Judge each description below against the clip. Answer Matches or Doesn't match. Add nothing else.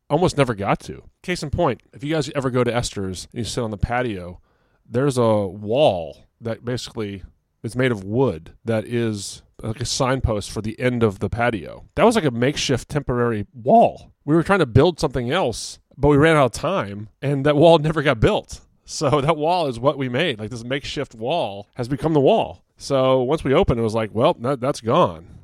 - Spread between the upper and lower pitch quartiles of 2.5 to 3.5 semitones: Doesn't match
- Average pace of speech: Doesn't match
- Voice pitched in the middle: Doesn't match